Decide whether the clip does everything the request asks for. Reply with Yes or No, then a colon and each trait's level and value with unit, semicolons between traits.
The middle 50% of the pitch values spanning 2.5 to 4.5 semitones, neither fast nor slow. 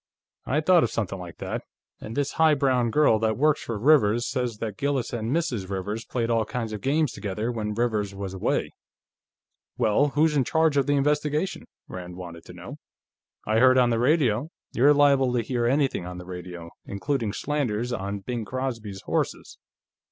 No: average, 5.3 semitones; average, 185 wpm